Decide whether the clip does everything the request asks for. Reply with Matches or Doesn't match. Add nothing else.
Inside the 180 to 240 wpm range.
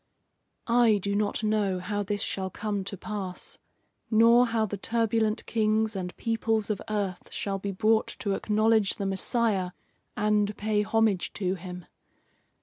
Doesn't match